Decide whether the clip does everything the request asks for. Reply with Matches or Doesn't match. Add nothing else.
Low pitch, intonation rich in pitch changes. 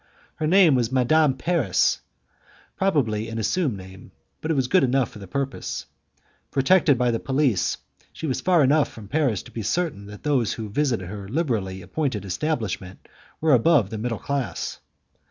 Matches